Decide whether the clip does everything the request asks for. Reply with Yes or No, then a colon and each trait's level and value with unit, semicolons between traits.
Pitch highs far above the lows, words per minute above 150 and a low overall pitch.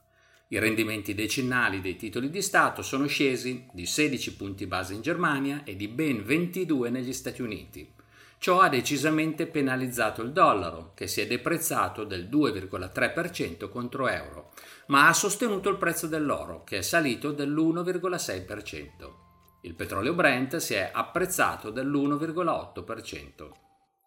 No: wide, 7.0 semitones; average, 130 wpm; low, 130 Hz